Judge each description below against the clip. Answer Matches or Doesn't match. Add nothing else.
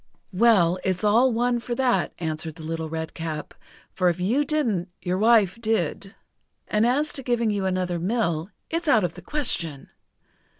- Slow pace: Doesn't match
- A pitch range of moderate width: Doesn't match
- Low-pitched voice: Doesn't match